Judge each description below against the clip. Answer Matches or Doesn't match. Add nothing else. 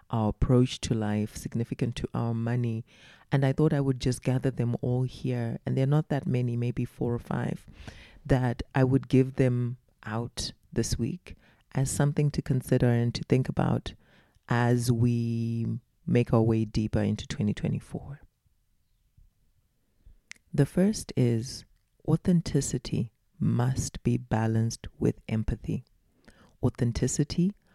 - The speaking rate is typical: Doesn't match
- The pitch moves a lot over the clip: Doesn't match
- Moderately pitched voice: Doesn't match